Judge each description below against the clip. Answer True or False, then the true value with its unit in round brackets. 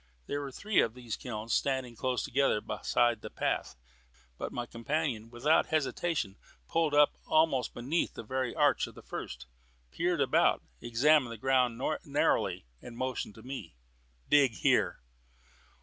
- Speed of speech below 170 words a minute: True (150 wpm)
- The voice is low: True (130 Hz)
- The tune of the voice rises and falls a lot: False (3.7 semitones)